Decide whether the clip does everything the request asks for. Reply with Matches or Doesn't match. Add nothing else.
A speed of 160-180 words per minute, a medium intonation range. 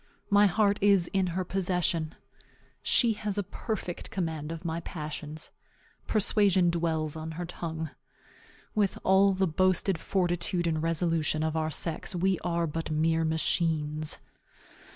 Doesn't match